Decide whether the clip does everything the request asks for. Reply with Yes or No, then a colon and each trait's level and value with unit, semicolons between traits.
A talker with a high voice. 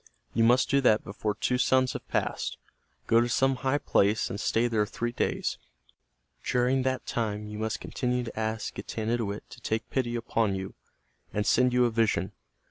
No: low, 115 Hz